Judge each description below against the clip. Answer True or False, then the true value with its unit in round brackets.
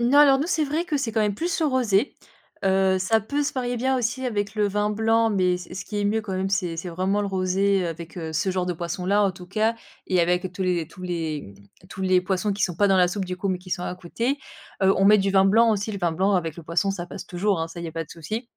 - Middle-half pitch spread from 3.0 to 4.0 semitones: True (3.4 semitones)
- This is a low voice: False (195 Hz)